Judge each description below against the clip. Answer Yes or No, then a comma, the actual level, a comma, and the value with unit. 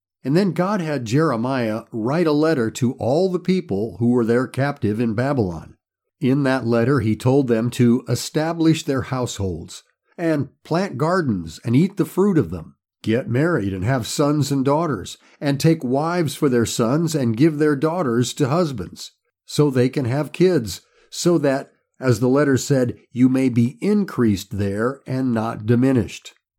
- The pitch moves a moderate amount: Yes, average, 4.5 semitones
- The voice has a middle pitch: No, low, 130 Hz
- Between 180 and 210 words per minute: No, average, 170 wpm